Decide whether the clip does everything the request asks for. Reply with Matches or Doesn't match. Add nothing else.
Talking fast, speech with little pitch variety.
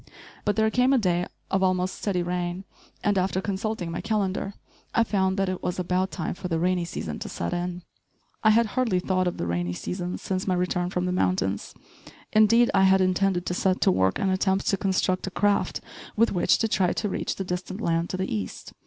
Matches